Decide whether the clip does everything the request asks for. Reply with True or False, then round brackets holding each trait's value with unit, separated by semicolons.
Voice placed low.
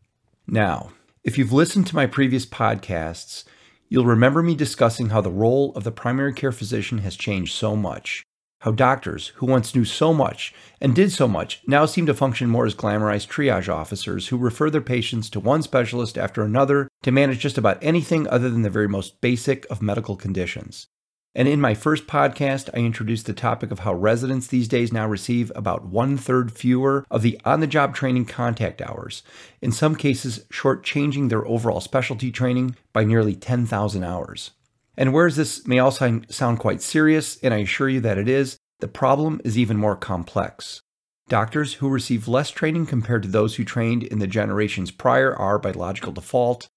True (120 Hz)